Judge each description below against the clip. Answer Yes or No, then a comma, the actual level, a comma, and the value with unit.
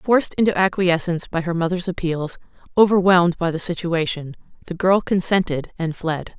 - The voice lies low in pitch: No, medium, 175 Hz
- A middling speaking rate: Yes, average, 150 wpm